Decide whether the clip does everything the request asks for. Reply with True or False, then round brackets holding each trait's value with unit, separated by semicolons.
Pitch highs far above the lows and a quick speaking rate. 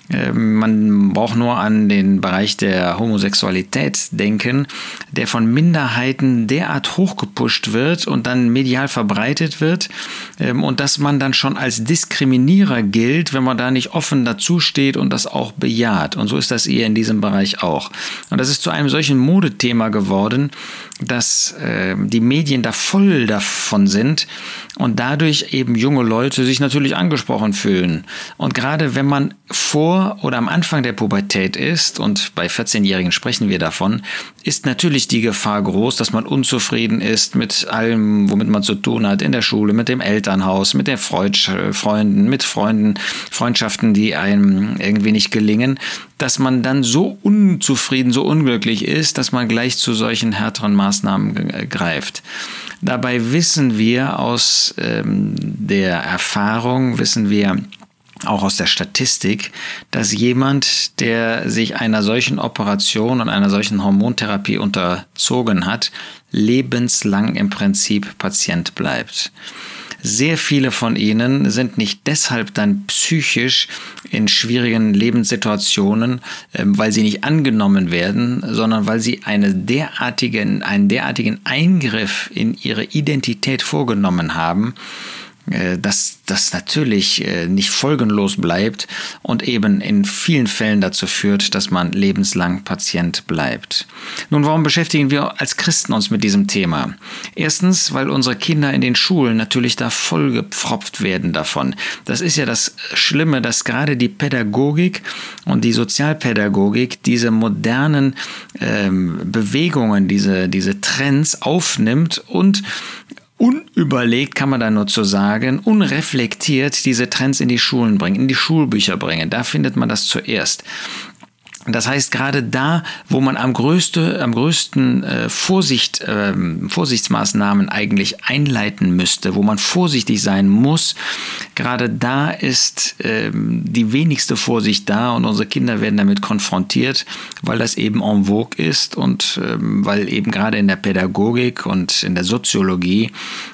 False (6.6 semitones; 140 wpm)